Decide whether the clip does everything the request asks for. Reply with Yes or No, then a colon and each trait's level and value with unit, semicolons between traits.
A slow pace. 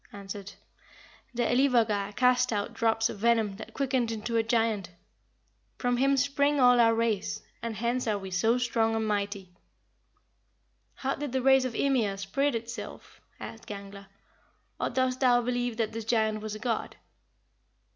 No: average, 155 wpm